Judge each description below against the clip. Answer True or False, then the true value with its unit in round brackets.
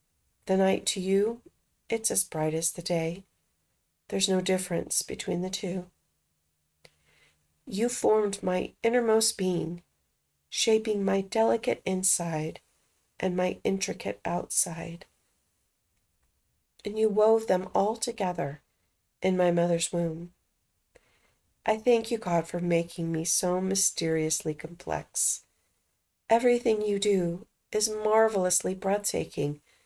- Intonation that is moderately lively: True (4.0 semitones)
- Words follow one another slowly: True (110 wpm)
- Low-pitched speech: False (185 Hz)